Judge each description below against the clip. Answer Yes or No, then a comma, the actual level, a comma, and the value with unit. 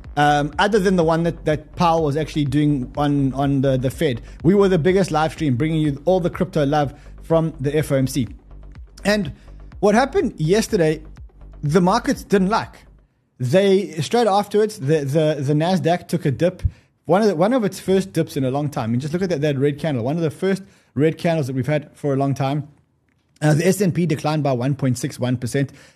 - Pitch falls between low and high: Yes, medium, 155 Hz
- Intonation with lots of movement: No, average, 4.4 semitones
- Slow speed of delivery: No, fast, 205 wpm